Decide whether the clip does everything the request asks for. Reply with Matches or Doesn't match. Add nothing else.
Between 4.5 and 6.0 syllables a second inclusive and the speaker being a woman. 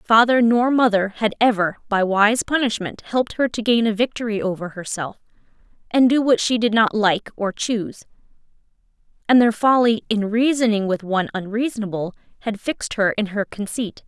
Matches